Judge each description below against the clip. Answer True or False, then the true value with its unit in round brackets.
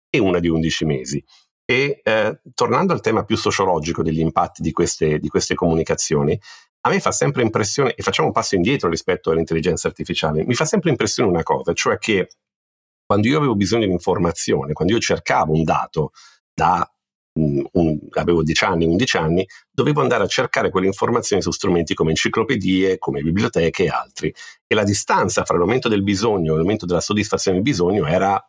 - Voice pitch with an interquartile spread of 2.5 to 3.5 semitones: False (3.9 semitones)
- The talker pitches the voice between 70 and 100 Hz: True (85 Hz)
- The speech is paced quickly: True (185 wpm)